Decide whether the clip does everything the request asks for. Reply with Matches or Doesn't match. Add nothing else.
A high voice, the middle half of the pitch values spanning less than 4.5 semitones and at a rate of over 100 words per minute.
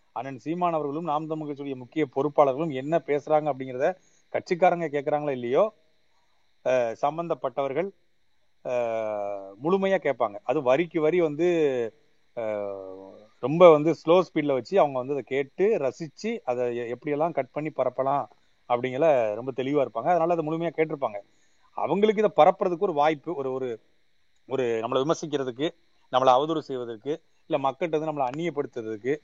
Doesn't match